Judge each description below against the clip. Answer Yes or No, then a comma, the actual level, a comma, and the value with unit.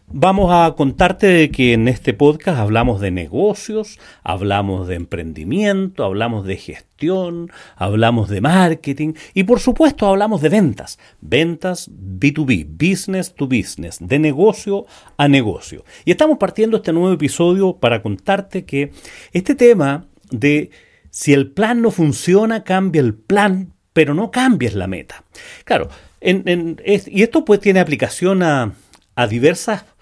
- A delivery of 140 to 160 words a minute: Yes, average, 145 wpm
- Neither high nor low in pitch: Yes, medium, 170 Hz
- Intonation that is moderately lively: No, wide, 7.0 semitones